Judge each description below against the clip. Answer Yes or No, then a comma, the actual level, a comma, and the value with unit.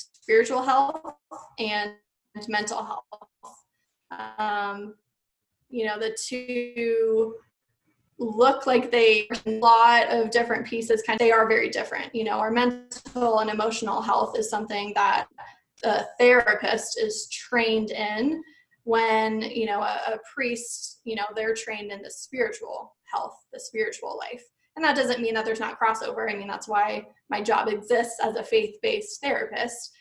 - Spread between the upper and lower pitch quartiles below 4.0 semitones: Yes, average, 2.7 semitones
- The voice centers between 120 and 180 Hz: No, high, 230 Hz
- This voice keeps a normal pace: Yes, average, 150 wpm